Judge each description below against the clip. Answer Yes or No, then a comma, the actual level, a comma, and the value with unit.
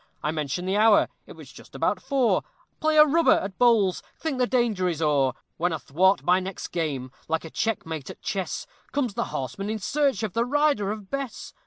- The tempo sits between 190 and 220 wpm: Yes, average, 200 wpm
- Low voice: No, high, 200 Hz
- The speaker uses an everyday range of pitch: No, wide, 7.0 semitones